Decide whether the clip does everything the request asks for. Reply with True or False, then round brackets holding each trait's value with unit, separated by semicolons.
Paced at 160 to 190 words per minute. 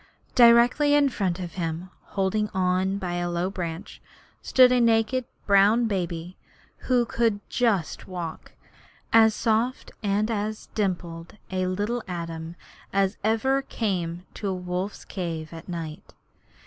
False (135 wpm)